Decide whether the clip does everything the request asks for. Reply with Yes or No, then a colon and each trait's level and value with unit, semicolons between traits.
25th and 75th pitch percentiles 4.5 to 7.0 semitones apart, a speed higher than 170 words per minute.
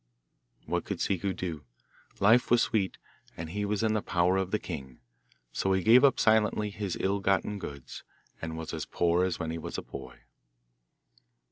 No: average, 3.7 semitones; average, 180 wpm